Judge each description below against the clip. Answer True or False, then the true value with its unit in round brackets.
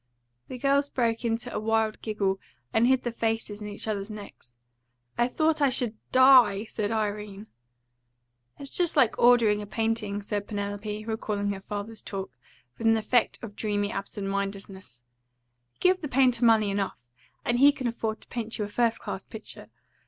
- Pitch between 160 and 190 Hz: False (220 Hz)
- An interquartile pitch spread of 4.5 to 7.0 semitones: False (2.8 semitones)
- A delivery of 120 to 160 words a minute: False (175 wpm)